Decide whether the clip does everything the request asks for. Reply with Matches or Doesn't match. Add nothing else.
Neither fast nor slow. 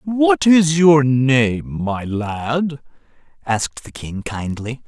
Doesn't match